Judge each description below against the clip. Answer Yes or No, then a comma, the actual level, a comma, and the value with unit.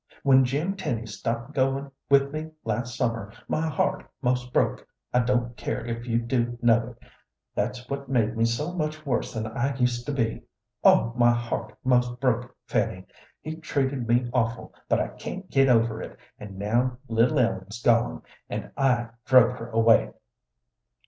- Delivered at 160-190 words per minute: Yes, average, 170 wpm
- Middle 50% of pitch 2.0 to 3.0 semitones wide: Yes, average, 2.7 semitones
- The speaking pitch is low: Yes, low, 120 Hz